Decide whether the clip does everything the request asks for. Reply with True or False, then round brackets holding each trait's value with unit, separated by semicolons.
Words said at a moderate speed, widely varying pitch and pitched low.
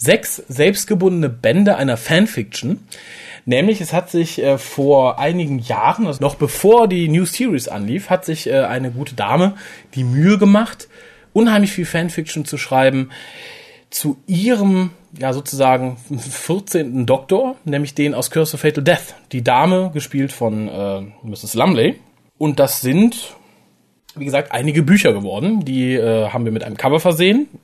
False (150 wpm; 6.0 semitones; 150 Hz)